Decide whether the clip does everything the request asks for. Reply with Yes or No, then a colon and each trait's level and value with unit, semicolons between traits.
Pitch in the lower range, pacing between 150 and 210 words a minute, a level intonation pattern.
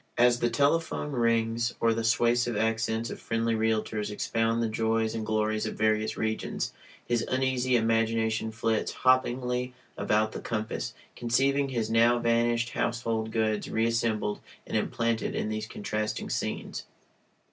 No: low, 115 Hz; slow, 135 wpm; narrow, 1.3 semitones